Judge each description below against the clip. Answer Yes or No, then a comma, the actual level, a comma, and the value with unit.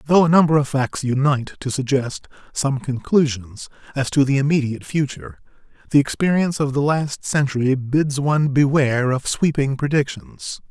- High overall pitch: No, medium, 140 Hz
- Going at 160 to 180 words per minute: No, average, 150 wpm